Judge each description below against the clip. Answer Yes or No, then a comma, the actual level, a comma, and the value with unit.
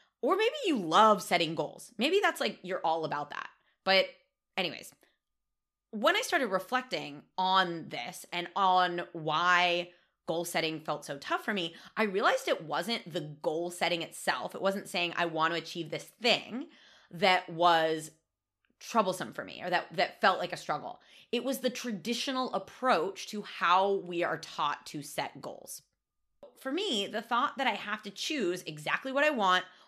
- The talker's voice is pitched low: No, medium, 185 Hz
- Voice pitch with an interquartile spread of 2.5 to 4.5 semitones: No, wide, 5.6 semitones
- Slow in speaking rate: No, average, 175 wpm